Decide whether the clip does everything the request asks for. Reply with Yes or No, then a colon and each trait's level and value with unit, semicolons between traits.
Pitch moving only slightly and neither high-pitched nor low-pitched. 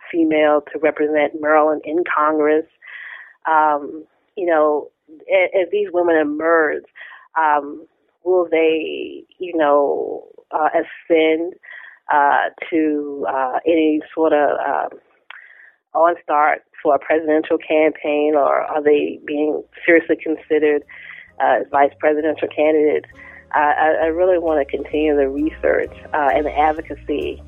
Yes: narrow, 1.8 semitones; medium, 155 Hz